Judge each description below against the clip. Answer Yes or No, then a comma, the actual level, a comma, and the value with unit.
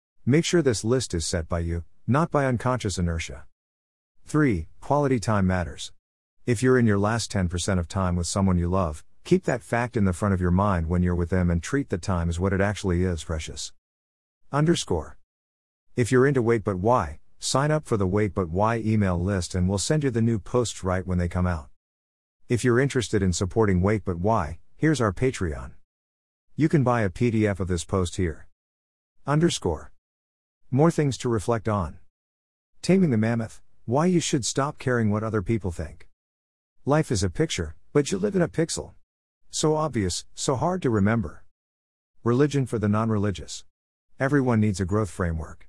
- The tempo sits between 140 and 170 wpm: No, average, 185 wpm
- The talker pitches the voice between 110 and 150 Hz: No, low, 100 Hz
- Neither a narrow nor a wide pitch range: No, wide, 6.4 semitones